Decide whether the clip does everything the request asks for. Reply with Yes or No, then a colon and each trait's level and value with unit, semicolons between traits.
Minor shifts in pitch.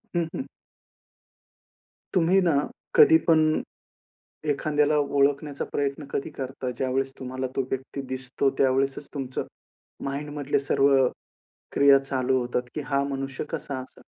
Yes: narrow, 1.9 semitones